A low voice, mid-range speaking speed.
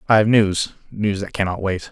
No: low, 100 Hz; fast, 220 wpm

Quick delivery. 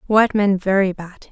No: average, 185 wpm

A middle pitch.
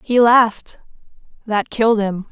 No: high, 220 Hz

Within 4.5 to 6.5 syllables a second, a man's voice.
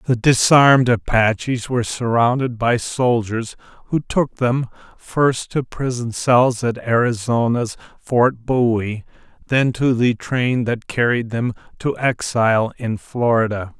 No: 3.9 syllables/s; male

